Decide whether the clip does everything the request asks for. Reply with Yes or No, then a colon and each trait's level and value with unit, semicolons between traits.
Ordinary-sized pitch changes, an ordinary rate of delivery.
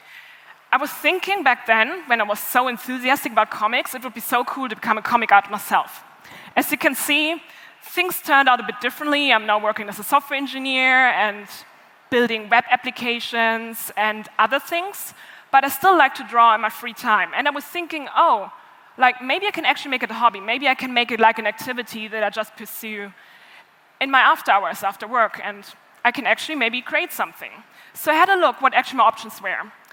No: average, 4.2 semitones; fast, 215 wpm